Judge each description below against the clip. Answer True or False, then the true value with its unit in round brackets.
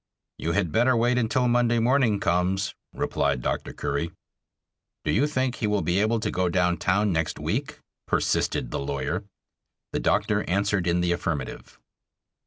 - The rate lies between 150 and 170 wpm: True (160 wpm)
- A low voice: True (100 Hz)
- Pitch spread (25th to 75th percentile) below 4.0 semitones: False (5.2 semitones)